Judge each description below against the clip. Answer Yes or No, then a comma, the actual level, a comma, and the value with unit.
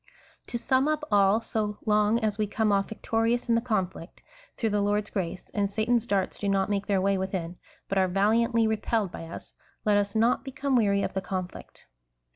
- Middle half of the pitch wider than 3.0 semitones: No, narrow, 2.5 semitones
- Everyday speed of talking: No, fast, 210 wpm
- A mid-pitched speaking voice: No, high, 210 Hz